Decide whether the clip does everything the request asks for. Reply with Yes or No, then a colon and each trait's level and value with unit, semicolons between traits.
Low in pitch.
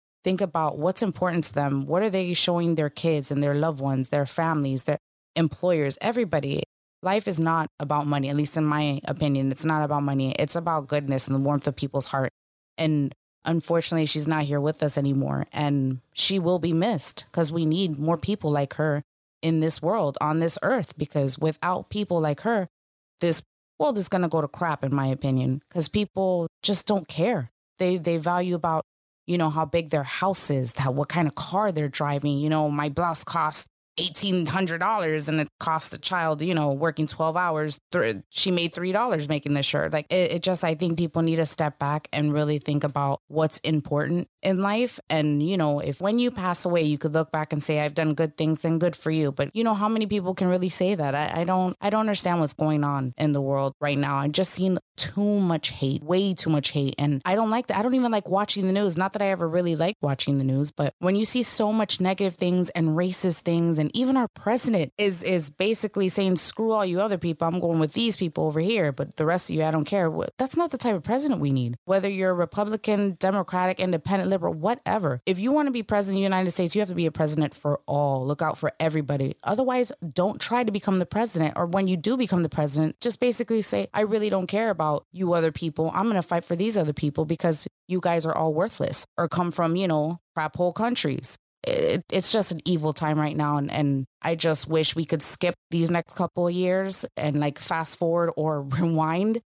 No: medium, 165 Hz